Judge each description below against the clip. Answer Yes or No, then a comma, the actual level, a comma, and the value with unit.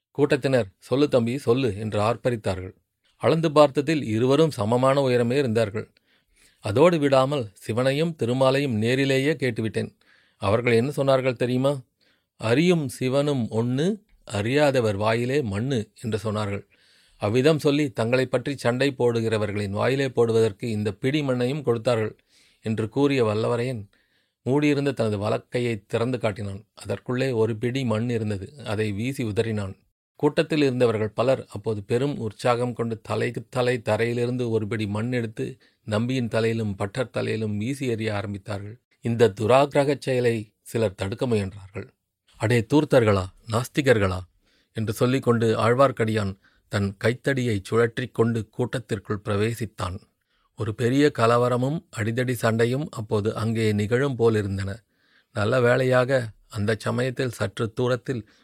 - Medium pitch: No, low, 115 Hz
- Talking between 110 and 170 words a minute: Yes, average, 115 wpm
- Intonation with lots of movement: No, average, 3.3 semitones